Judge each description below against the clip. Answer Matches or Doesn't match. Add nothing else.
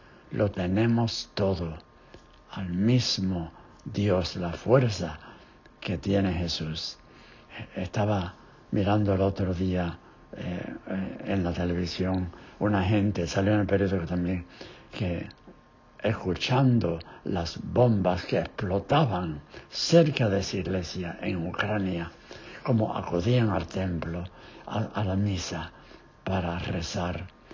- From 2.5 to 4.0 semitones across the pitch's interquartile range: Matches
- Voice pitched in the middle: Doesn't match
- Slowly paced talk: Matches